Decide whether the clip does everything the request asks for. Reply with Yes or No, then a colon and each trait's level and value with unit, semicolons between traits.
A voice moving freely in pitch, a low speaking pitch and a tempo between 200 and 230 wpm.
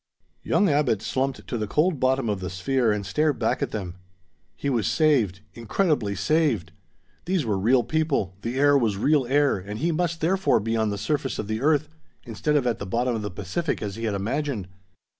Yes: wide, 6.2 semitones; low, 120 Hz; fast, 205 wpm